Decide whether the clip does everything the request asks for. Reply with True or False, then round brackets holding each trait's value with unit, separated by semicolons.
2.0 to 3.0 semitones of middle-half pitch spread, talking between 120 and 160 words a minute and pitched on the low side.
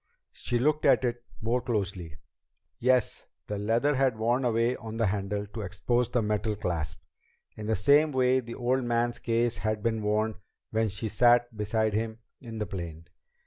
False (2.5 semitones; 175 wpm; 115 Hz)